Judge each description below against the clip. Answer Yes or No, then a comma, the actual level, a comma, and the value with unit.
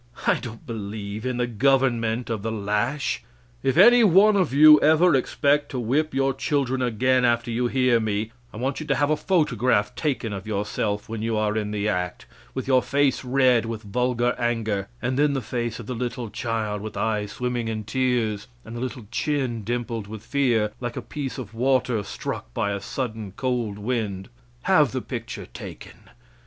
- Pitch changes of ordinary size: Yes, average, 3.4 semitones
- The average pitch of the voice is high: No, low, 120 Hz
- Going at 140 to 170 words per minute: No, average, 190 wpm